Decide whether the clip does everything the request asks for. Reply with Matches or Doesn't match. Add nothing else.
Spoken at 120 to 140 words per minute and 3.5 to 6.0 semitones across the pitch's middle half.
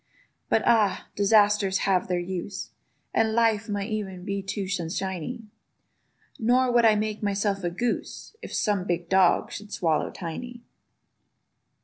Doesn't match